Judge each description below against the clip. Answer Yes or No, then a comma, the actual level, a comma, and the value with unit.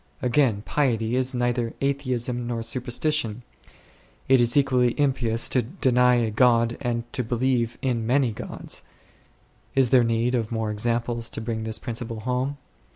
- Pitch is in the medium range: No, low, 120 Hz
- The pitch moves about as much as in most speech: No, narrow, 1.9 semitones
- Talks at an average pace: Yes, average, 150 wpm